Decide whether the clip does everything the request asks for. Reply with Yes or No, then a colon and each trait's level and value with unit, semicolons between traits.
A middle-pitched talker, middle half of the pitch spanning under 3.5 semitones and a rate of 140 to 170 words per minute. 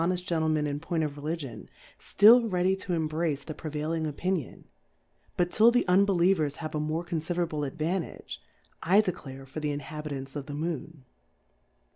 Yes: medium, 160 Hz; average, 3.1 semitones; average, 160 wpm